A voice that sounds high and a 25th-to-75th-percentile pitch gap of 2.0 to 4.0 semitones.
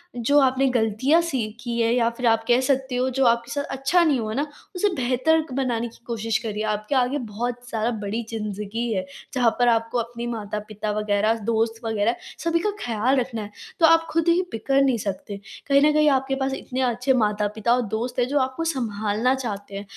Yes: high, 240 Hz; average, 3.4 semitones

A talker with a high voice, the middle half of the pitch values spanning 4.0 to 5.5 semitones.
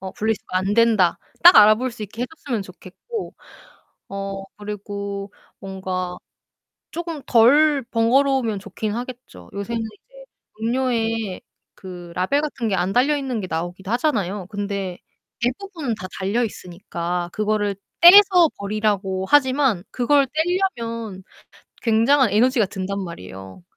Yes: high, 215 Hz; average, 5.1 semitones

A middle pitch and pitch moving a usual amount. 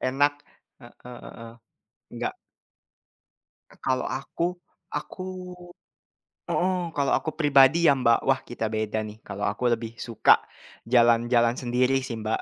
No: low, 125 Hz; average, 3.0 semitones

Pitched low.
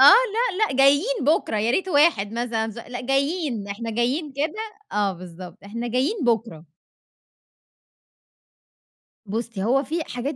No: high, 245 Hz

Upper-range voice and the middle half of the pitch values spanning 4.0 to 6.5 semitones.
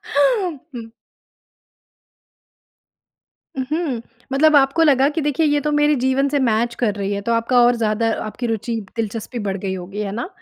Yes: high, 245 Hz; average, 4.6 semitones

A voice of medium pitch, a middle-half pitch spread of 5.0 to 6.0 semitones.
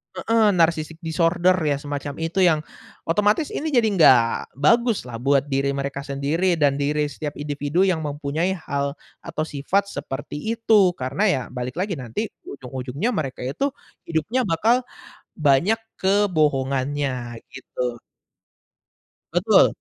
Yes: medium, 150 Hz; wide, 5.4 semitones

